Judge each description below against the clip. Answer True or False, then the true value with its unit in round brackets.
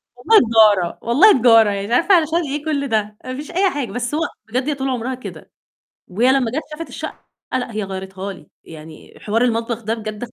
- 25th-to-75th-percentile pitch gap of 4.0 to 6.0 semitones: True (4.9 semitones)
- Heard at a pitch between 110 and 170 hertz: False (240 Hz)